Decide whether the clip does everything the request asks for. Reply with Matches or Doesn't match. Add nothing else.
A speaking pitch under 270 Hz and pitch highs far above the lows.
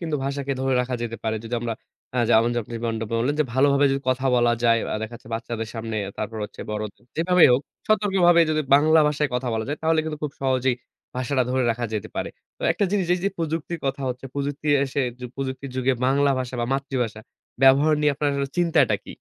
Doesn't match